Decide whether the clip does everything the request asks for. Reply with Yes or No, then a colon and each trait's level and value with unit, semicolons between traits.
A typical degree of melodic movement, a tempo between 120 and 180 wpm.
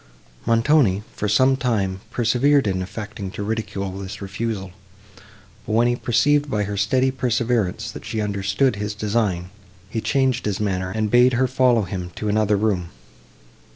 Yes: average, 3.6 semitones; average, 155 wpm